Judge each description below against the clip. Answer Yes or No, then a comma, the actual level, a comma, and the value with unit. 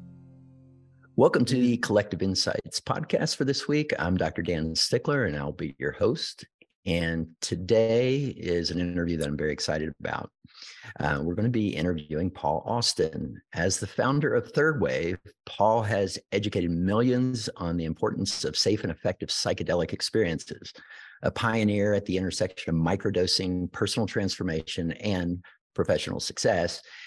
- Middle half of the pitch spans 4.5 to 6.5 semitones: Yes, average, 5.2 semitones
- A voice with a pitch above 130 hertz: No, very low, 95 Hz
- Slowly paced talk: No, average, 150 wpm